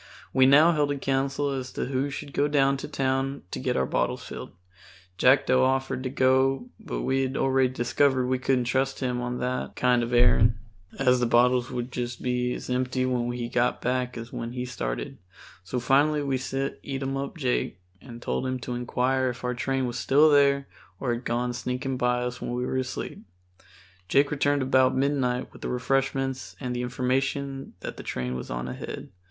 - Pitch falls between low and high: No, low, 130 Hz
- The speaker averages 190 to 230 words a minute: Yes, average, 195 wpm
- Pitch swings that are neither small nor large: No, narrow, 1.6 semitones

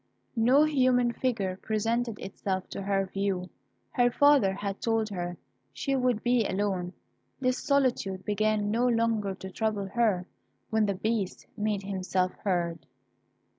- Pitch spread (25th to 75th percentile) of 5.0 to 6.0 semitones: No, average, 3.8 semitones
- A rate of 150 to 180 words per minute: No, slow, 135 wpm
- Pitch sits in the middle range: No, high, 210 Hz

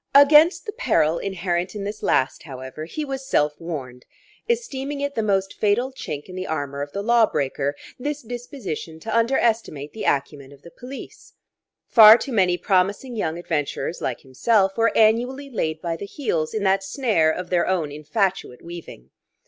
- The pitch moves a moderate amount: No, wide, 7.2 semitones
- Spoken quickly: No, average, 170 wpm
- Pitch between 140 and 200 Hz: Yes, high, 190 Hz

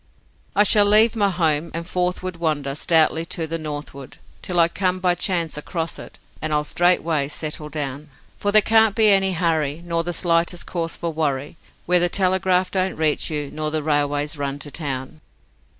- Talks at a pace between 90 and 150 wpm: No, average, 180 wpm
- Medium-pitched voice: Yes, medium, 165 Hz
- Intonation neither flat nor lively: Yes, average, 3.3 semitones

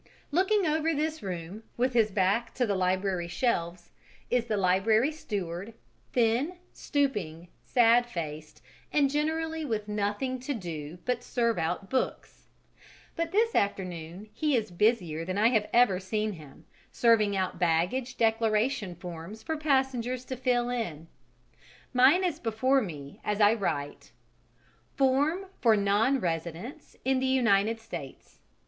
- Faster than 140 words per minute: No, slow, 135 wpm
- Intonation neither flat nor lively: No, wide, 6.1 semitones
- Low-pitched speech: No, high, 225 Hz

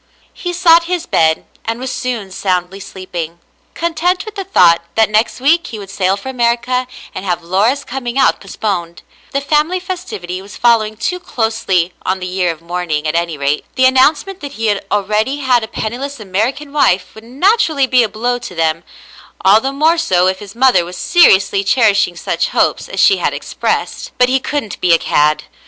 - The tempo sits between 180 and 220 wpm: Yes, average, 190 wpm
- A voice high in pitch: Yes, high, 220 Hz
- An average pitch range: No, wide, 6.8 semitones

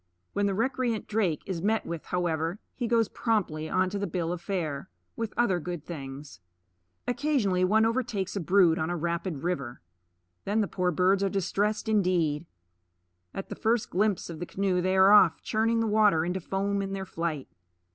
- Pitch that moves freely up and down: No, average, 3.8 semitones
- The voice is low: No, high, 190 Hz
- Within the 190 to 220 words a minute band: No, average, 180 wpm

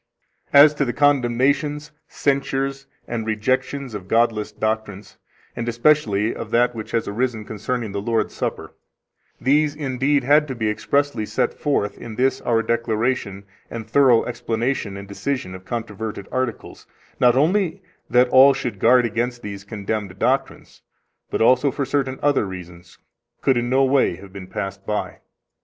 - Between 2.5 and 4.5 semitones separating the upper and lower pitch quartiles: Yes, average, 4.2 semitones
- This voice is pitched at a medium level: No, low, 120 Hz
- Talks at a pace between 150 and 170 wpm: Yes, average, 155 wpm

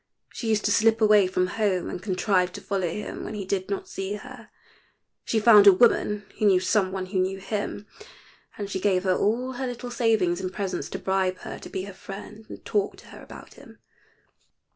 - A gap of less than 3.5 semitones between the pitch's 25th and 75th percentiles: Yes, narrow, 2.5 semitones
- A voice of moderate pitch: No, high, 200 Hz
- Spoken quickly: Yes, fast, 210 wpm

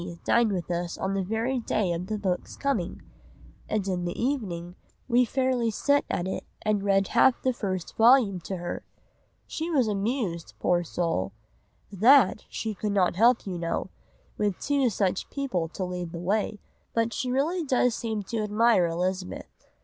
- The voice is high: Yes, high, 205 Hz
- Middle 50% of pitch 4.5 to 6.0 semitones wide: Yes, average, 5.1 semitones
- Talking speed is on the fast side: No, average, 170 wpm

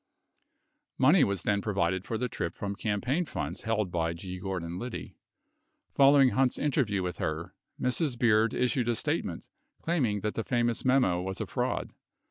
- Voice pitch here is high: No, low, 110 Hz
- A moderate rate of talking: Yes, average, 170 wpm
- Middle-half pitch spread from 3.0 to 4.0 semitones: No, average, 5.2 semitones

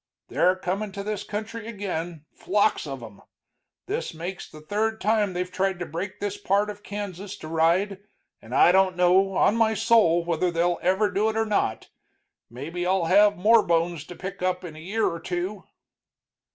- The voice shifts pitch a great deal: No, average, 3.2 semitones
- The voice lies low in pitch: No, medium, 185 Hz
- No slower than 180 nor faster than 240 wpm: Yes, average, 185 wpm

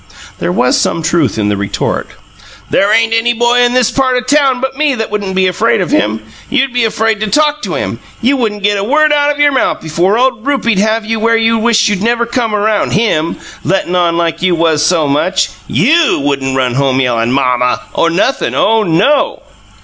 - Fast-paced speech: Yes, fast, 215 wpm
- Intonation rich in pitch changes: Yes, wide, 6.7 semitones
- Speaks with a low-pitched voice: No, high, 215 Hz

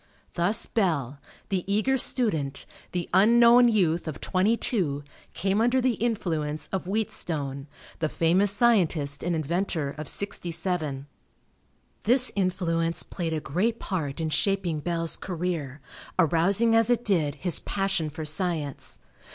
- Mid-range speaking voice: Yes, medium, 175 Hz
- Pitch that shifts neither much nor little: Yes, average, 4.6 semitones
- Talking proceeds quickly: No, slow, 135 wpm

